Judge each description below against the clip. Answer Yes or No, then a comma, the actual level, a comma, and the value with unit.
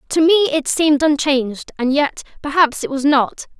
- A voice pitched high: Yes, very high, 290 Hz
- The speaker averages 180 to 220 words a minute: No, average, 150 wpm